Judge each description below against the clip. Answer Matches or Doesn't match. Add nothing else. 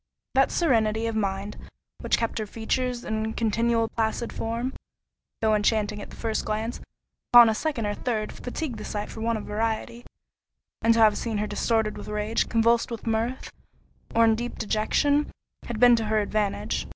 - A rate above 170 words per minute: Matches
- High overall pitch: Matches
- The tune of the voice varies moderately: Doesn't match